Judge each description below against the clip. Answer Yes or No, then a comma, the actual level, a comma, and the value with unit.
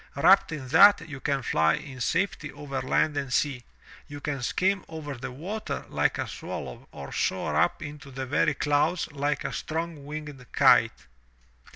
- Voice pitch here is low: No, medium, 145 Hz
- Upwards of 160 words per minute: Yes, average, 170 wpm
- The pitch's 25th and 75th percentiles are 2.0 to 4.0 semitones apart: Yes, average, 2.9 semitones